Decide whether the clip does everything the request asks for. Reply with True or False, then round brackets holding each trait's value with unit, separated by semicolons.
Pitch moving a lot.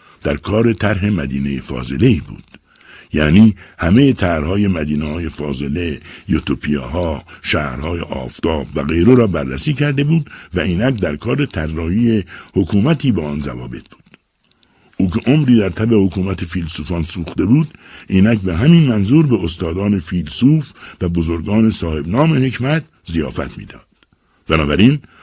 True (6.4 semitones)